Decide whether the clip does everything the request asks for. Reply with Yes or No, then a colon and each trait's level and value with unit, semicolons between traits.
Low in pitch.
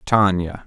Yes: very low, 95 Hz